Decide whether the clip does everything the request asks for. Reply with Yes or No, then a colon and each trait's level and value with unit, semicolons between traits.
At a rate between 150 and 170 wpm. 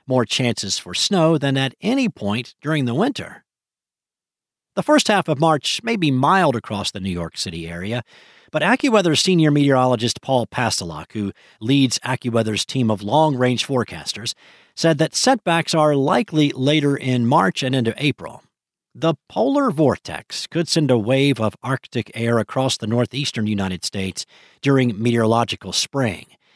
Yes: average, 155 wpm